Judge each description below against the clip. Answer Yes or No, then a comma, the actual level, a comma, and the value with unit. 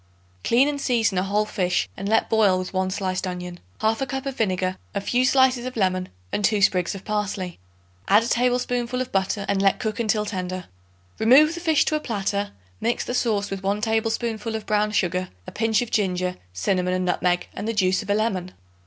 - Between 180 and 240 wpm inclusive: Yes, fast, 205 wpm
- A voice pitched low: No, high, 210 Hz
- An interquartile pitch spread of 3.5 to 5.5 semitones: Yes, average, 3.9 semitones